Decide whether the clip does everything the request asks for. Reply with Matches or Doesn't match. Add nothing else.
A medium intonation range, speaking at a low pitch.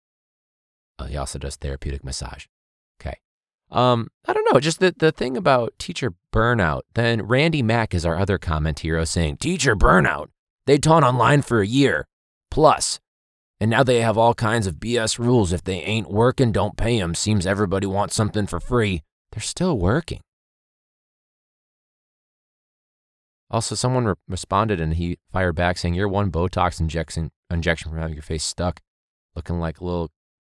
Doesn't match